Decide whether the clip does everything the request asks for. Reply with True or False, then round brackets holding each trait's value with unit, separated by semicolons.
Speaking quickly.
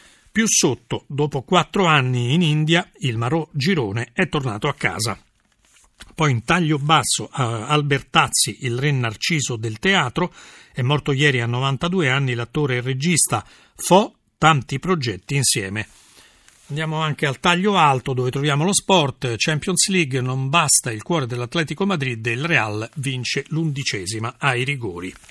False (145 wpm)